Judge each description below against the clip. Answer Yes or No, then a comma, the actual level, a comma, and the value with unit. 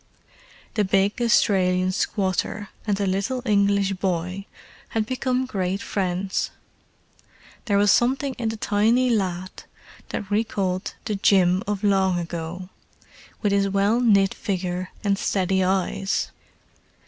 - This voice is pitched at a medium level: No, high, 195 Hz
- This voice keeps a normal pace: No, slow, 125 wpm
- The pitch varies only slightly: Yes, narrow, 2.1 semitones